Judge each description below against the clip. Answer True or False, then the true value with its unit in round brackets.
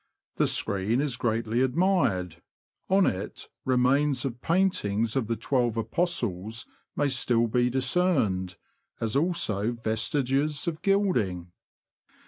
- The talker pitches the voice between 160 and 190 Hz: False (125 Hz)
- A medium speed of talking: False (115 wpm)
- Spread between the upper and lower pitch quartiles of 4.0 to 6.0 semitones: True (5.1 semitones)